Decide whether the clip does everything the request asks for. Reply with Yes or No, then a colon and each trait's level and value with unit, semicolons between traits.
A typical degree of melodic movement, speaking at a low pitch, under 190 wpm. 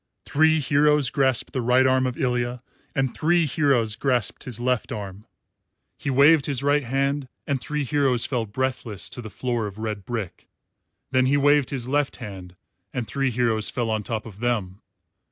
Yes: average, 3.6 semitones; low, 125 Hz; average, 175 wpm